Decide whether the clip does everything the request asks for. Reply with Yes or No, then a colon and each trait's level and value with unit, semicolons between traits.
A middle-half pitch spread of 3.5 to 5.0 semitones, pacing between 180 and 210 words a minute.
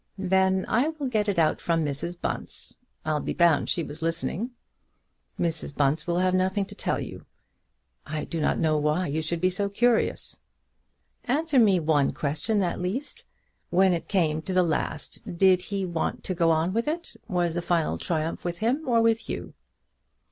Yes: average, 4.0 semitones; average, 185 wpm